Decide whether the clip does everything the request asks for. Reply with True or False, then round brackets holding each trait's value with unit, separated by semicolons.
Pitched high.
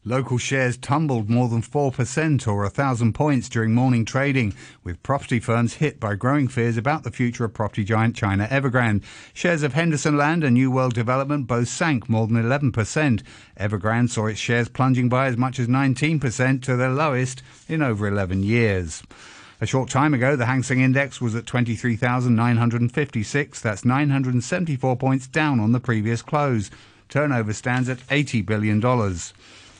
False (125 Hz)